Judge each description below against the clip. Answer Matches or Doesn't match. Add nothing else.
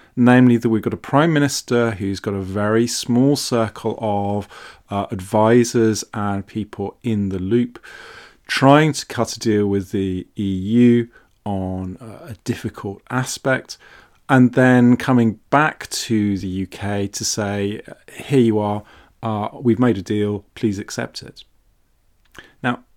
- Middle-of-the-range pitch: Doesn't match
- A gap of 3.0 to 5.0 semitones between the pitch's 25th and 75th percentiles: Matches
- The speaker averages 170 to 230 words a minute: Doesn't match